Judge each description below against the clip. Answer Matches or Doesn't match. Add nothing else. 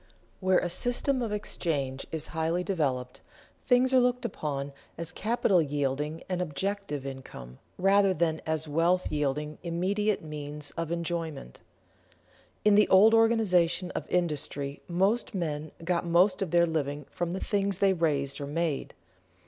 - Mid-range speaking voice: Matches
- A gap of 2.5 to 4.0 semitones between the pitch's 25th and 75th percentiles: Doesn't match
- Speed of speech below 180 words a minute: Matches